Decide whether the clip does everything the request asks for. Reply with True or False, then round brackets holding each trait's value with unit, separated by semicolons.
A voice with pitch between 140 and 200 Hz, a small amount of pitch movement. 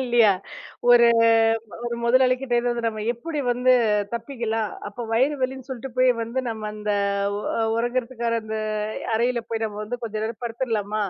False (235 Hz; 2.1 semitones)